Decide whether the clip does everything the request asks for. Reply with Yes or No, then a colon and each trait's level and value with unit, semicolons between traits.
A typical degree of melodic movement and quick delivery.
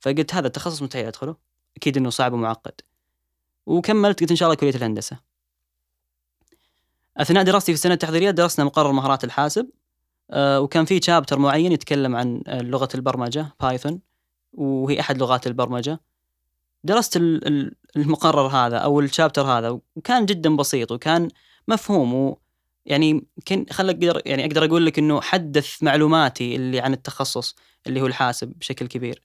Yes: average, 4.8 semitones; fast, 140 wpm